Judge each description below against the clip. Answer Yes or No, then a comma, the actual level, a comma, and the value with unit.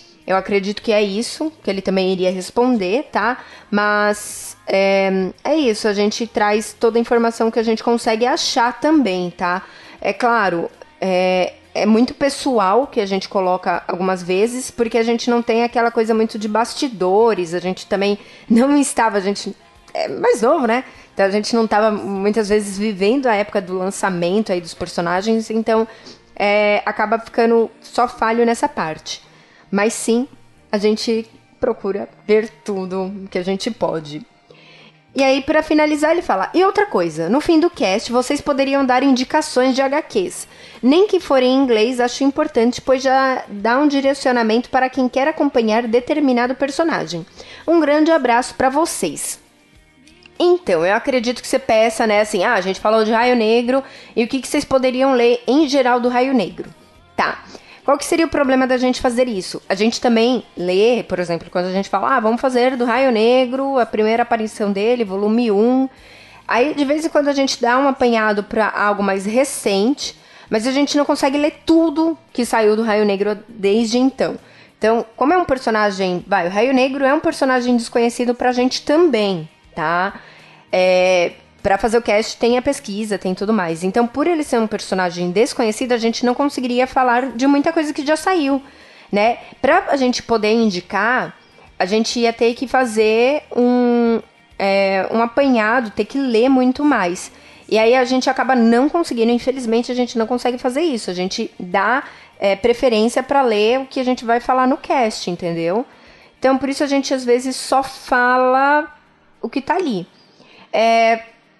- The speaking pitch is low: No, high, 235 Hz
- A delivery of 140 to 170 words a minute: No, average, 180 wpm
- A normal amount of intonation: Yes, average, 4.1 semitones